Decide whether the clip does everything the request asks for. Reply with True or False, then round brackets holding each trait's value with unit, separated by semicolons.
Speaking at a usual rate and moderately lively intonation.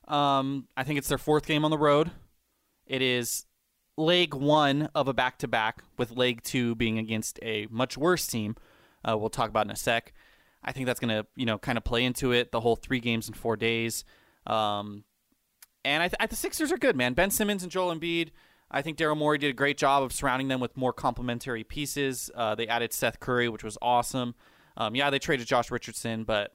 False (220 wpm; 4.1 semitones)